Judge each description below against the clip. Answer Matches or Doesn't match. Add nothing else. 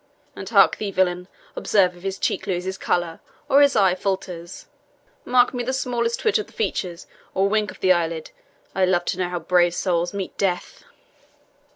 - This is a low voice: Doesn't match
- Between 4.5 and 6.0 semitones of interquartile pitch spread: Doesn't match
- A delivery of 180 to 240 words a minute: Matches